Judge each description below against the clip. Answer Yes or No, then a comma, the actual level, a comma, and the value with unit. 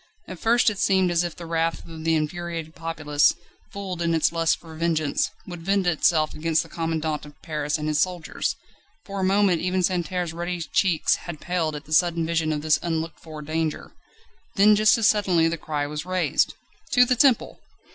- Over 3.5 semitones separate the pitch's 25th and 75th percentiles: No, narrow, 2.6 semitones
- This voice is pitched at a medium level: Yes, medium, 165 Hz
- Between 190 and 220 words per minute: Yes, average, 195 wpm